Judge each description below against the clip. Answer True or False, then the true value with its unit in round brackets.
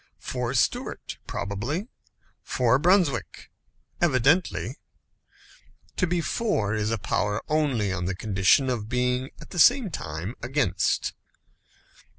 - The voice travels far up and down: True (6.9 semitones)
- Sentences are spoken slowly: True (115 wpm)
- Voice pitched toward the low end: True (125 Hz)